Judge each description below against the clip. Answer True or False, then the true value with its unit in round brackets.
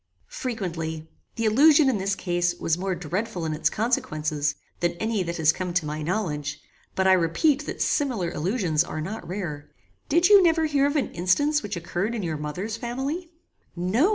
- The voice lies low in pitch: False (185 Hz)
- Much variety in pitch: True (6.8 semitones)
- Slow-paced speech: False (180 wpm)